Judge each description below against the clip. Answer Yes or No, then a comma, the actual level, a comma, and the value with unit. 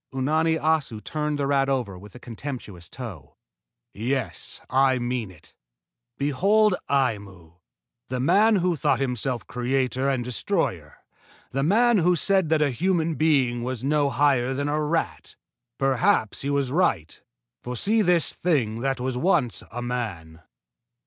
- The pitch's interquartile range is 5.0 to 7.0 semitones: No, average, 4.3 semitones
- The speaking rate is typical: Yes, average, 145 wpm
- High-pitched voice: No, low, 135 Hz